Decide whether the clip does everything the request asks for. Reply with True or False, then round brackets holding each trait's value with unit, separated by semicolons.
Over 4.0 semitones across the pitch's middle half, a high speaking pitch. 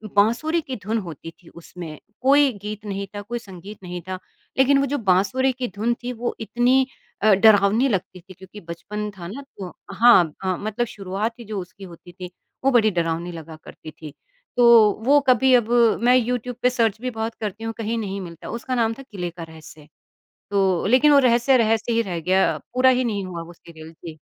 True (5.1 semitones; 210 Hz)